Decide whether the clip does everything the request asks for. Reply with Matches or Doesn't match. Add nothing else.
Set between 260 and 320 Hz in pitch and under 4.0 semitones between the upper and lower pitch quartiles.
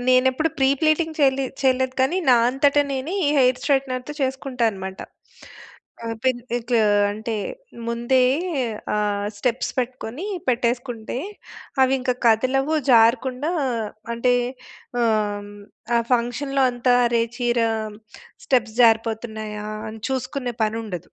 Doesn't match